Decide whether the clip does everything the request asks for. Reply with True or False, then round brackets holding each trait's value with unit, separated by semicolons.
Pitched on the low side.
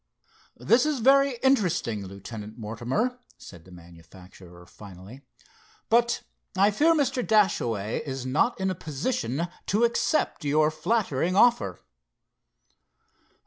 False (155 Hz)